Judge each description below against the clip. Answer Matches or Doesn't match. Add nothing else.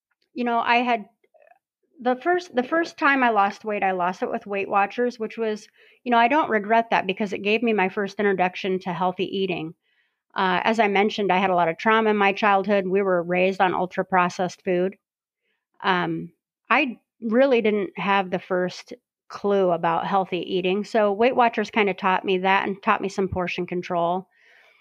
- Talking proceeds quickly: Doesn't match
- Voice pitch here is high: Matches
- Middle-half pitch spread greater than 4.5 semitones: Doesn't match